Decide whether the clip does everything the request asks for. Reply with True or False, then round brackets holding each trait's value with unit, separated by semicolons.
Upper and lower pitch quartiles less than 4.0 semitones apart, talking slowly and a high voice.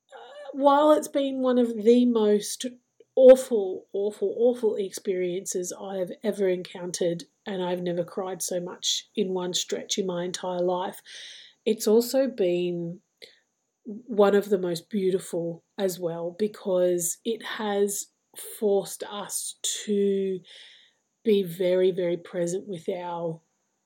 False (5.2 semitones; 125 wpm; 200 Hz)